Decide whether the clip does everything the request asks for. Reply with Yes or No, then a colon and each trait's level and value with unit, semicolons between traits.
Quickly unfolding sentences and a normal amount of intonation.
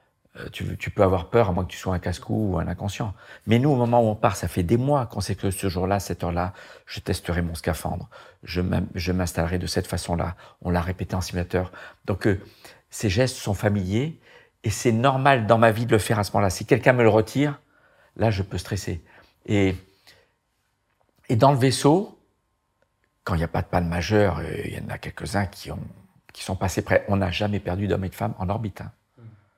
Yes: fast, 225 wpm; average, 3.9 semitones